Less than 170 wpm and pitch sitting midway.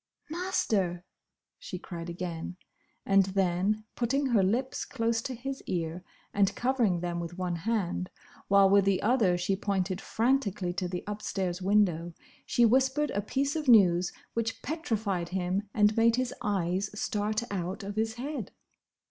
No: average, 150 wpm; high, 200 Hz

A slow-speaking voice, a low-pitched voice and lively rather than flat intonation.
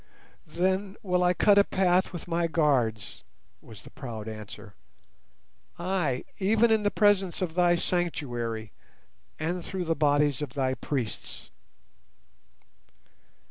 No: slow, 125 wpm; medium, 165 Hz; wide, 6.4 semitones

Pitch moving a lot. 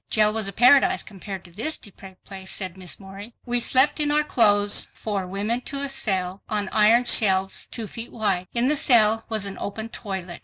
No: average, 3.6 semitones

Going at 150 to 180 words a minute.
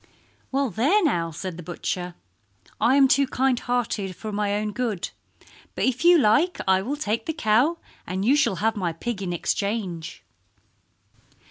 Yes: average, 165 wpm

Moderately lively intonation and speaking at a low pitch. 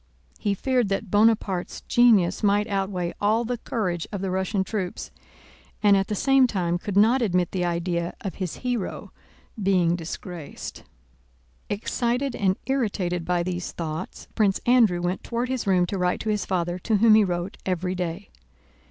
No: average, 3.6 semitones; high, 195 Hz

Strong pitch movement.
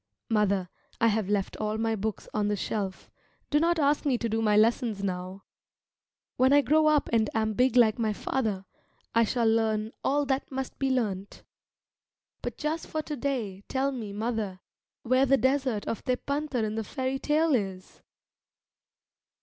No: average, 4.2 semitones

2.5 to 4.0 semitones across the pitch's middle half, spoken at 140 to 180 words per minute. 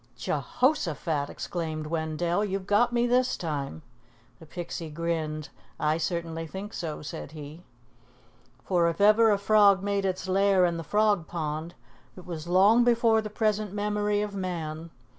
No: average, 4.4 semitones; average, 155 wpm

